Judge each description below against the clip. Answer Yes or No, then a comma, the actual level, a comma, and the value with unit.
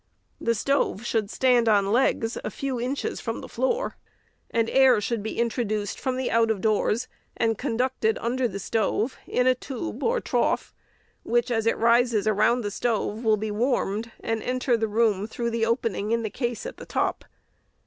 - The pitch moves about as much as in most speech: No, narrow, 2.3 semitones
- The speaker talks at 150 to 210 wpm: Yes, average, 185 wpm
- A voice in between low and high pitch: No, high, 230 Hz